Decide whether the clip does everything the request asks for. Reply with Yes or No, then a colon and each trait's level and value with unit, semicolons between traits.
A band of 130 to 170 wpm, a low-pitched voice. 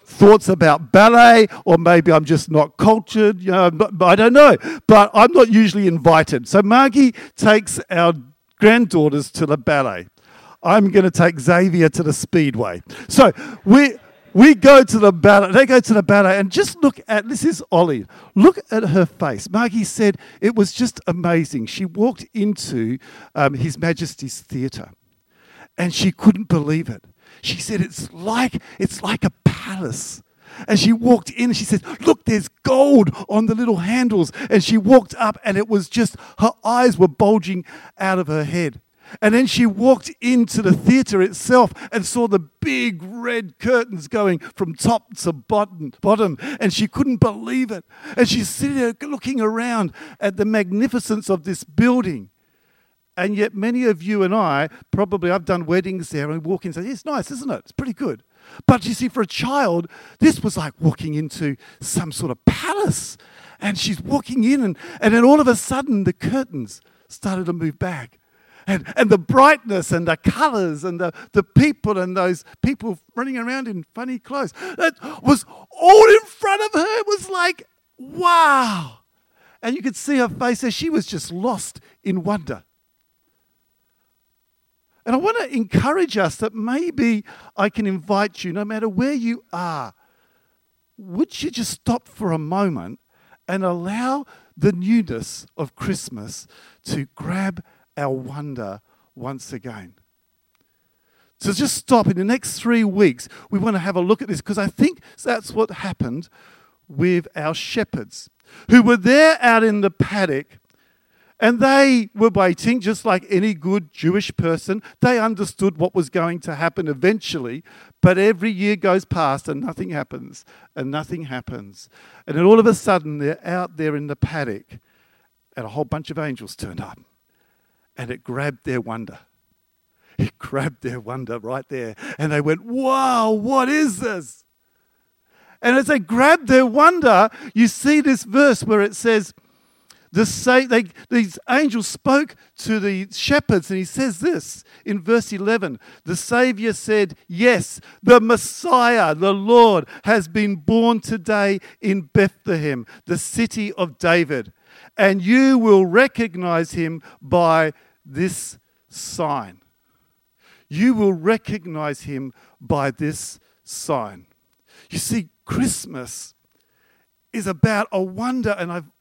No: average, 160 wpm; high, 205 Hz